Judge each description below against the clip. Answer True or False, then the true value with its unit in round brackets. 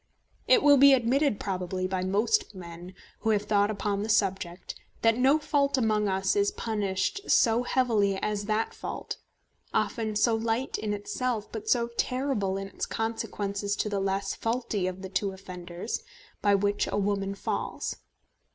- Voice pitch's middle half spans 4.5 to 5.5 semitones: False (3.2 semitones)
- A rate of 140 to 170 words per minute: True (160 wpm)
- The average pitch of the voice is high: True (210 Hz)